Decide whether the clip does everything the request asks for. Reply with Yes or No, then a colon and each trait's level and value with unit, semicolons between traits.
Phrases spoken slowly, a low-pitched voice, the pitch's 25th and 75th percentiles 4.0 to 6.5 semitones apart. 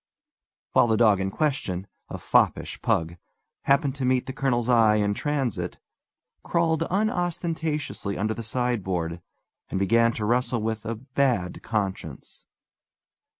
Yes: slow, 130 wpm; low, 115 Hz; average, 4.8 semitones